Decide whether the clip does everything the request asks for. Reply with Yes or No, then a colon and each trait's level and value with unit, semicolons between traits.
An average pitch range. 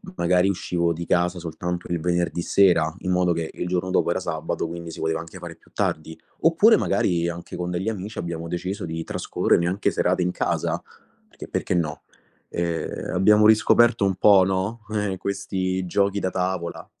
No: narrow, 2.2 semitones